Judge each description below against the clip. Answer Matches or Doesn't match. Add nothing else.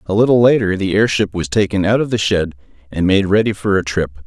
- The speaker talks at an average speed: Doesn't match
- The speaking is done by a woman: Doesn't match